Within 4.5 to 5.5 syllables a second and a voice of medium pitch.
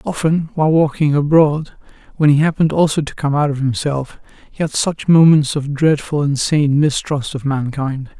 Yes: 4.9 syllables/s; medium, 145 Hz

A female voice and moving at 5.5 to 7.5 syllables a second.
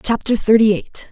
No: female; 5.0 syllables/s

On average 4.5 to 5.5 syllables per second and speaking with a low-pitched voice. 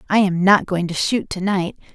No: 5.1 syllables/s; high, 190 Hz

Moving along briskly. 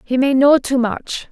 Yes: fast, 230 wpm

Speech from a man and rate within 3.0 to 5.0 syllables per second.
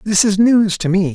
Yes: male; 4.6 syllables/s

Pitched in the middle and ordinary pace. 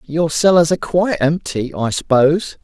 Yes: medium, 155 Hz; average, 160 wpm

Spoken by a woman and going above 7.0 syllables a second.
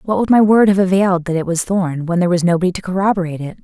Yes: female; 7.3 syllables/s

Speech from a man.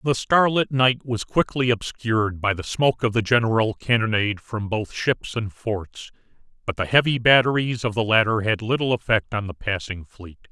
Yes: male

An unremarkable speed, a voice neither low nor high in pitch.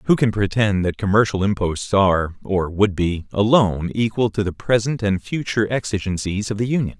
No: average, 180 wpm; low, 100 Hz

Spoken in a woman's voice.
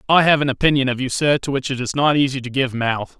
No: male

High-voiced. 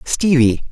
No: medium, 145 Hz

